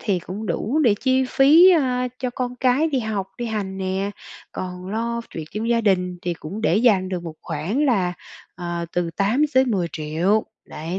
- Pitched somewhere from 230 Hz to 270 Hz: No, high, 205 Hz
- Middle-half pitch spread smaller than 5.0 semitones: No, wide, 5.6 semitones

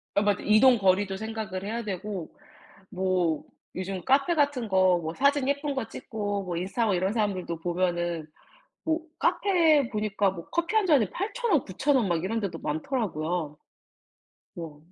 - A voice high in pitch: Yes, high, 205 Hz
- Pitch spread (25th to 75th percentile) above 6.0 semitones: Yes, wide, 6.6 semitones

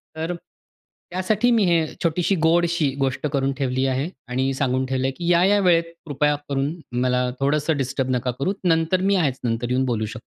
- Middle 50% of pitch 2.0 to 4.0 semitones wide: No, average, 4.7 semitones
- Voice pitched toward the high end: No, medium, 145 Hz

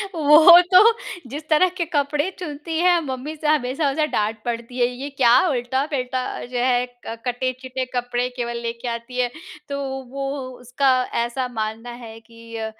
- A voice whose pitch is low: No, very high, 255 Hz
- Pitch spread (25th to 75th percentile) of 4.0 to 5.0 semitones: No, average, 3.4 semitones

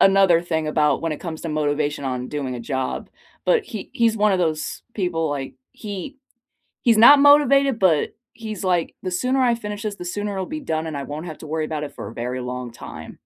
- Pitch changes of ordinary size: No, wide, 6.3 semitones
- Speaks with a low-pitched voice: No, medium, 170 Hz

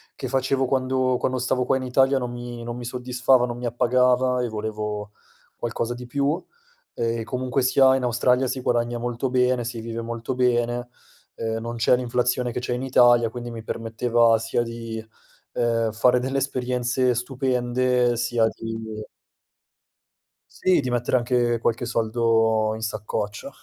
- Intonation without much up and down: Yes, narrow, 1.6 semitones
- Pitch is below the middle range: Yes, low, 120 Hz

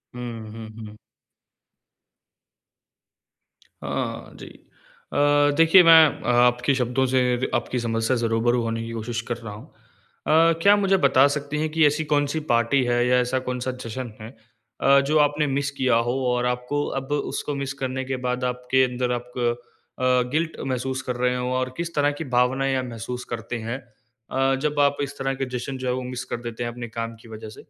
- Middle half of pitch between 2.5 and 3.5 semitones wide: Yes, average, 2.8 semitones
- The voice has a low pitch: Yes, low, 125 Hz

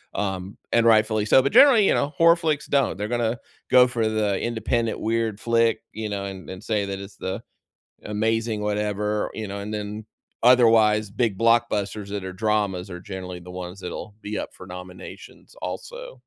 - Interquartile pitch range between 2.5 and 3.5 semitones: Yes, average, 2.8 semitones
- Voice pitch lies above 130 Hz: No, low, 105 Hz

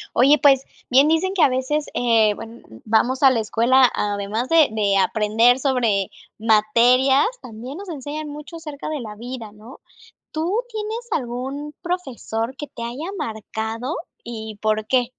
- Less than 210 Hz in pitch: No, very high, 250 Hz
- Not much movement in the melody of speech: No, average, 4.8 semitones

